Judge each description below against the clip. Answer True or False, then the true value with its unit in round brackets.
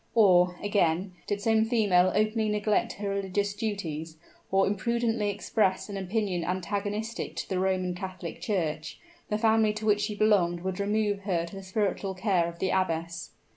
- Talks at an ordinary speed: True (165 wpm)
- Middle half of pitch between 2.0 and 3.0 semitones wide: True (2.7 semitones)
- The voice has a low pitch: False (200 Hz)